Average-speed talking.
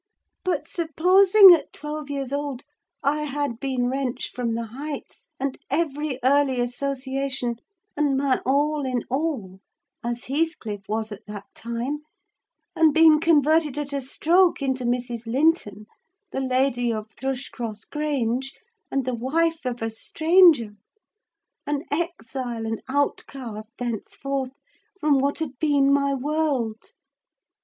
No: slow, 130 wpm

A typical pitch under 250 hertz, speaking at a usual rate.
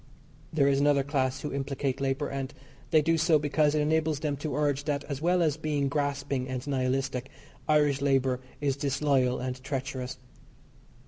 Yes: medium, 140 Hz; average, 170 wpm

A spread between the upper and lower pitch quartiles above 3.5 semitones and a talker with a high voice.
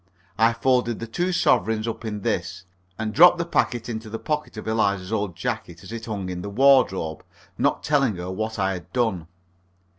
No: average, 4.1 semitones; low, 110 Hz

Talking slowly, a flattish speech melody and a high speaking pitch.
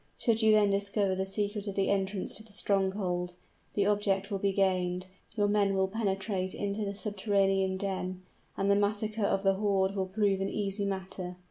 No: average, 190 wpm; narrow, 1.2 semitones; high, 195 Hz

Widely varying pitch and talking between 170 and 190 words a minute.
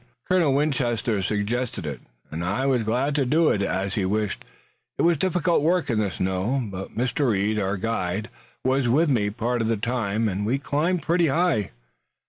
Yes: wide, 5.7 semitones; average, 180 wpm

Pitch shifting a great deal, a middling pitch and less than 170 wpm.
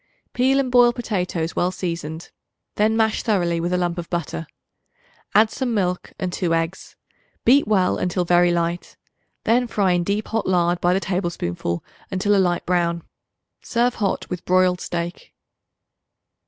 No: average, 3.5 semitones; medium, 180 Hz; average, 155 wpm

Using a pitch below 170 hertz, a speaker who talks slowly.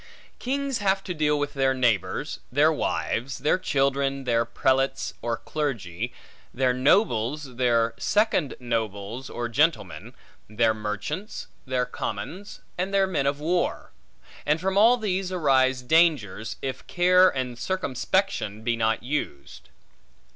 Yes: low, 135 Hz; slow, 130 wpm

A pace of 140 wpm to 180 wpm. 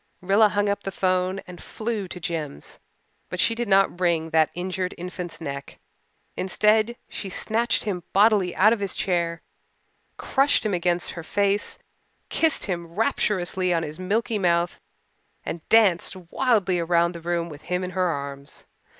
Yes: average, 160 wpm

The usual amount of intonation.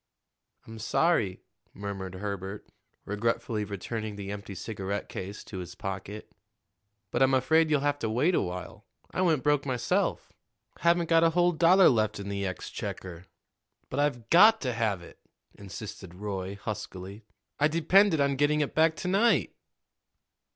No: wide, 7.6 semitones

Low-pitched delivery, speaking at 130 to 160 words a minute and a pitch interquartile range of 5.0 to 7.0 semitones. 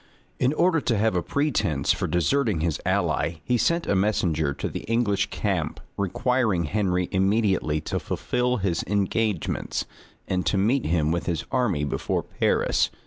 Yes: low, 100 Hz; average, 155 wpm; wide, 5.6 semitones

